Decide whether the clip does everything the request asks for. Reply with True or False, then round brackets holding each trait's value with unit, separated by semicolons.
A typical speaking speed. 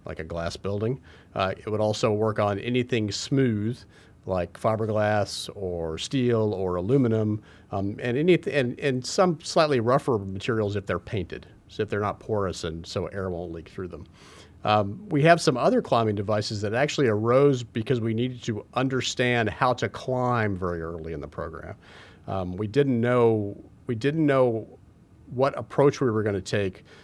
True (175 wpm)